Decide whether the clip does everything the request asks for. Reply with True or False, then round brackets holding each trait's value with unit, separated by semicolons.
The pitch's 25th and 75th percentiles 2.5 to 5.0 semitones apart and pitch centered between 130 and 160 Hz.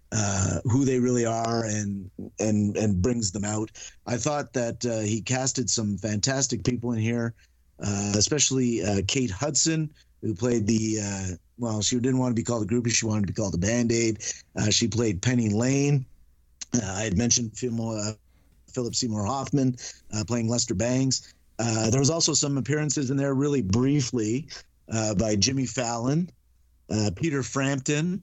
False (3.7 semitones; 115 Hz)